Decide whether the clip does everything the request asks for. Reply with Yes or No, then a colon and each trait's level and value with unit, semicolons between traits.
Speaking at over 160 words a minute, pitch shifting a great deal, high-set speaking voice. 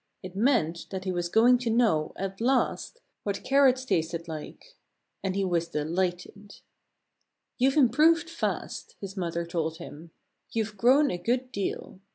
No: average, 150 wpm; wide, 6.4 semitones; high, 195 Hz